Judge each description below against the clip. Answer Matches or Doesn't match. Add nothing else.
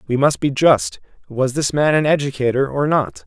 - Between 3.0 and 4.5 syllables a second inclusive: Doesn't match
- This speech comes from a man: Matches